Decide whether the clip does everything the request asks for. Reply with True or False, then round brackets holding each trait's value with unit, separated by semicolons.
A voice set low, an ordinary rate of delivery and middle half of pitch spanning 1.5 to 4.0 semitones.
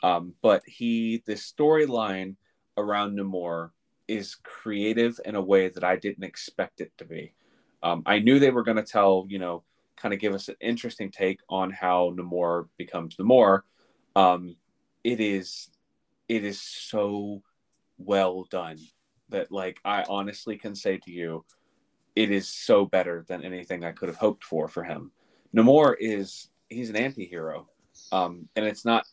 True (100 Hz; 165 wpm; 3.0 semitones)